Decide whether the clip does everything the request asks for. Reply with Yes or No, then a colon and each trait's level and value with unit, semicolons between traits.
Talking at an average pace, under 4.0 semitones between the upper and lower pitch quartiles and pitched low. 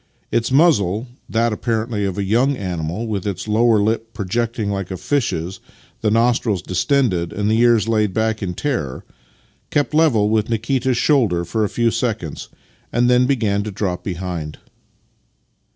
Yes: average, 170 wpm; average, 3.4 semitones; low, 110 Hz